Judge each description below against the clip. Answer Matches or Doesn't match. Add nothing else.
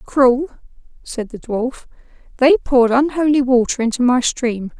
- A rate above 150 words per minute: Doesn't match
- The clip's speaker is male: Doesn't match